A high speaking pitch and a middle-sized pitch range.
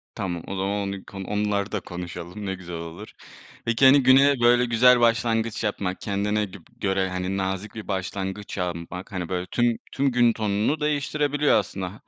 No: low, 100 Hz; average, 4.0 semitones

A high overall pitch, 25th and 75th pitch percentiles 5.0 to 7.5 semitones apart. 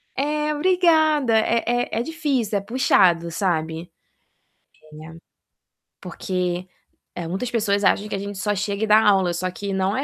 Yes: high, 205 Hz; wide, 5.5 semitones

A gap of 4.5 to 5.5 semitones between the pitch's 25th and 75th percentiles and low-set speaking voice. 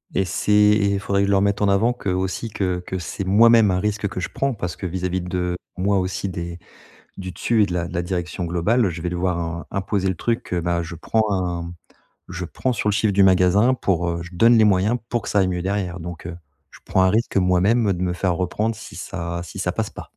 No: average, 2.8 semitones; very low, 95 Hz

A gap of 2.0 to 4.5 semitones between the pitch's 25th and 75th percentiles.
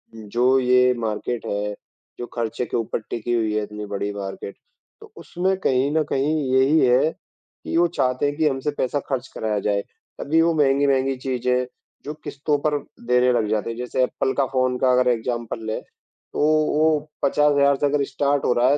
Yes: average, 3.4 semitones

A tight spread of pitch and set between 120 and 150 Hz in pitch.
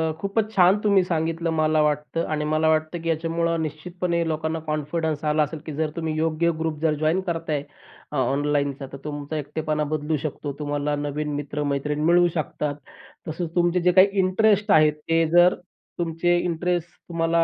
No: narrow, 2.1 semitones; medium, 160 Hz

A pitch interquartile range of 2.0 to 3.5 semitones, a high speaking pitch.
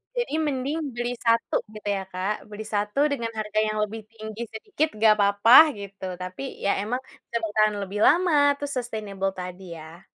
Yes: average, 3.2 semitones; high, 215 Hz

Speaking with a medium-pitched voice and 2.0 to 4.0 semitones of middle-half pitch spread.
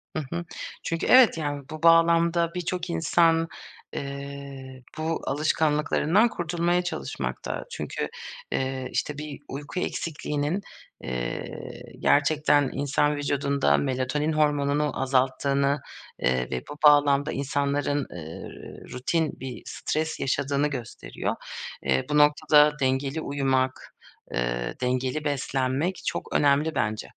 Yes: medium, 145 Hz; average, 2.8 semitones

